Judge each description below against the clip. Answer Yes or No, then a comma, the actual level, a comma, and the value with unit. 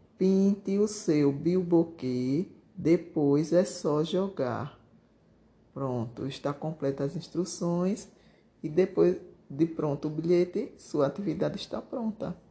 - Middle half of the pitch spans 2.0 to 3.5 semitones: No, average, 4.4 semitones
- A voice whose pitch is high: No, medium, 170 Hz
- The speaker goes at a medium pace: No, slow, 110 wpm